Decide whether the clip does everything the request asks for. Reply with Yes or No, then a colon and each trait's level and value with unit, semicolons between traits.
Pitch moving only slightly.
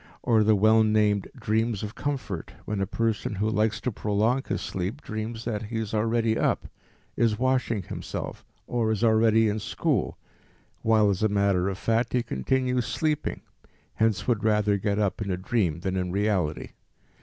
Yes: narrow, 2.2 semitones